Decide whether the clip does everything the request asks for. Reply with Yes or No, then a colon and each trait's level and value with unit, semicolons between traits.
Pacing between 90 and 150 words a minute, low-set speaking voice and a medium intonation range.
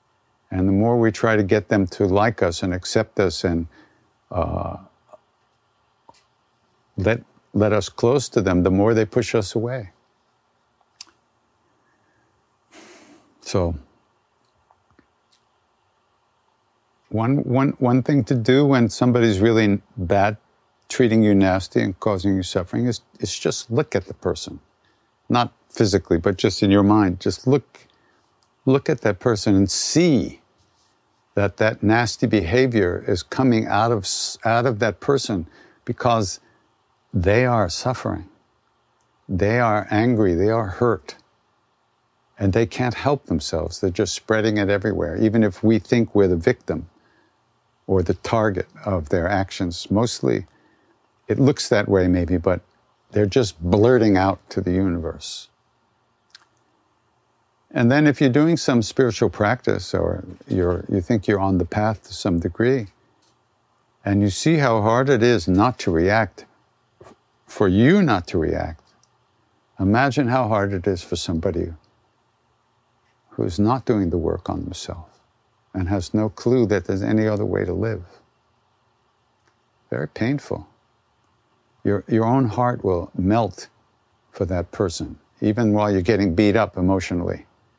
Yes: average, 140 wpm; low, 105 Hz; average, 3.6 semitones